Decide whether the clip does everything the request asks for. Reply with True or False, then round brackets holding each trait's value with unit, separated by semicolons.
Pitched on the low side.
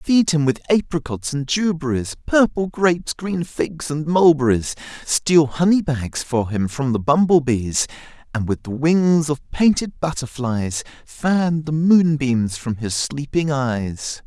False (145 Hz)